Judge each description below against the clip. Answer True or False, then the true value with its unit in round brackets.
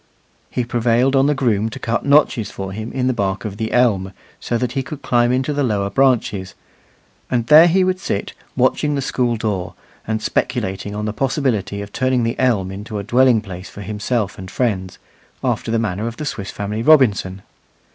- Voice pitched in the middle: False (115 Hz)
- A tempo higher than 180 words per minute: True (195 wpm)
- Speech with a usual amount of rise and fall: True (4.2 semitones)